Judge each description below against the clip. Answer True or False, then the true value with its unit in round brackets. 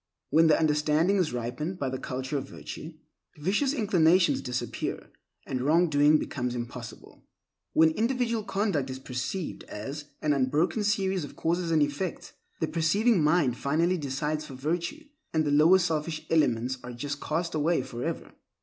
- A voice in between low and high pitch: True (155 Hz)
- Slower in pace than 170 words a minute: True (155 wpm)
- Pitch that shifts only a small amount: False (4.6 semitones)